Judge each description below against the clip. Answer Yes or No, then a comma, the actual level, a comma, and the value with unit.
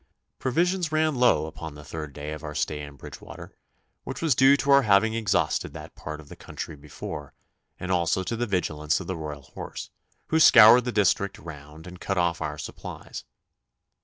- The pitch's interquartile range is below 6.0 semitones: No, wide, 8.0 semitones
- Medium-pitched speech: No, very low, 90 Hz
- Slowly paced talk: No, average, 190 wpm